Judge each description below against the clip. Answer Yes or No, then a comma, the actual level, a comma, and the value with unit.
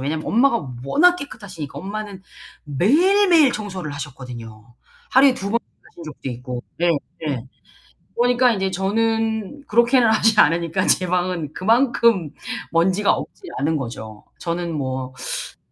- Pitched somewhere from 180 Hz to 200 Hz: Yes, medium, 185 Hz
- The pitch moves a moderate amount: No, wide, 7.7 semitones